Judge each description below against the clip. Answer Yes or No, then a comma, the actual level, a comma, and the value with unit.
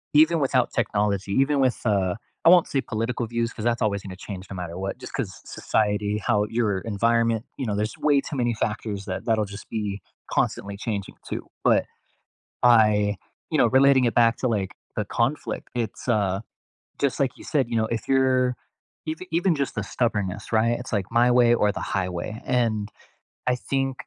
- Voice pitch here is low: Yes, low, 115 Hz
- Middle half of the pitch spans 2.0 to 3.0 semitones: No, average, 3.5 semitones